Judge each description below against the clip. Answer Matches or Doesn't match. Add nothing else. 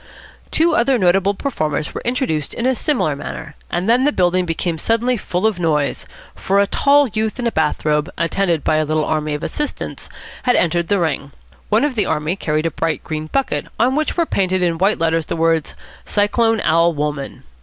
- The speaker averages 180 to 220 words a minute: Matches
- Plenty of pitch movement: Matches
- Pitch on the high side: Doesn't match